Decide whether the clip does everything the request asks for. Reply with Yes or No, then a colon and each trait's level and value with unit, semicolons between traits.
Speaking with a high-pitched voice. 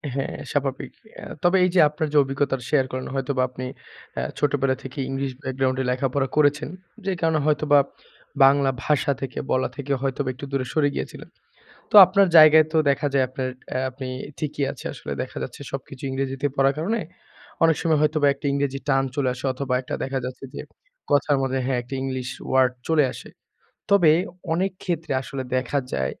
No: medium, 140 Hz